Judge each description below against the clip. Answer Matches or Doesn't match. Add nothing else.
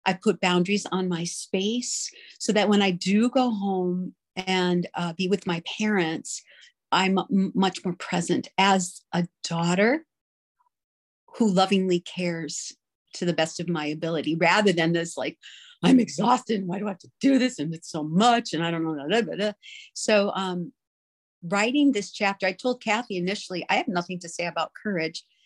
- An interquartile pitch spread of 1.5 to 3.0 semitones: Doesn't match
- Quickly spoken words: Doesn't match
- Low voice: Doesn't match